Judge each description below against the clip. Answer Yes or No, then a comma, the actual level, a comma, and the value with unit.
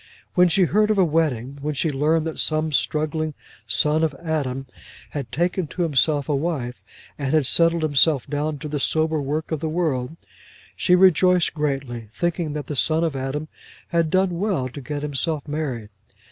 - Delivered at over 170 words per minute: Yes, average, 180 wpm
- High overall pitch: No, medium, 155 Hz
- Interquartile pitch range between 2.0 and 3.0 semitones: Yes, average, 2.7 semitones